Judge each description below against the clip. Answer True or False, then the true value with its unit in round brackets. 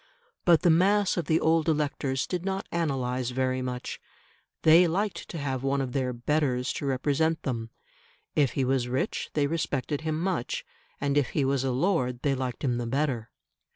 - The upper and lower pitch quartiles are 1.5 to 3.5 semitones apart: False (3.9 semitones)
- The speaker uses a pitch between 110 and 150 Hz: True (140 Hz)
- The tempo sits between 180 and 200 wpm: True (185 wpm)